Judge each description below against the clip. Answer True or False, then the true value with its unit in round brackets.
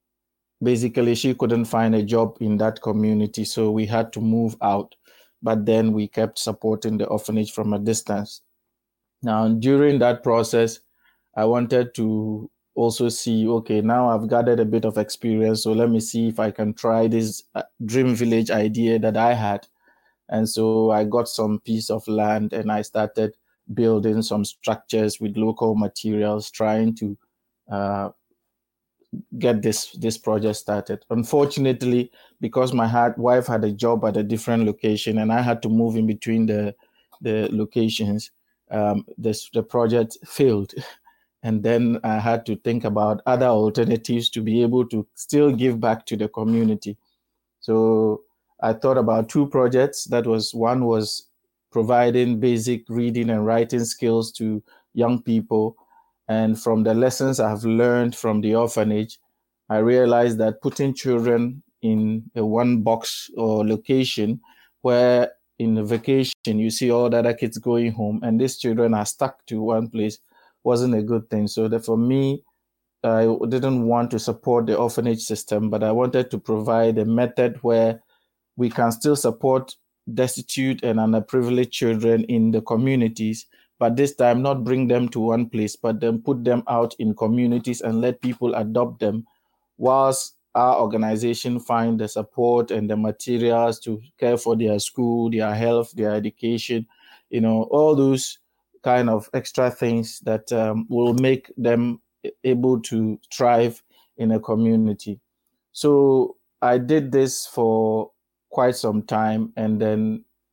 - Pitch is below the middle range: True (115 Hz)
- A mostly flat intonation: True (1.7 semitones)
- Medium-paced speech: True (160 wpm)